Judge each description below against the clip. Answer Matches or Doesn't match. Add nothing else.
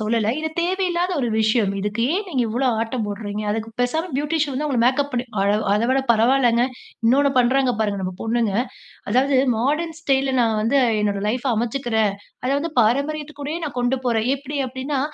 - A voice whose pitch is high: Matches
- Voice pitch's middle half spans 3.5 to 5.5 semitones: Matches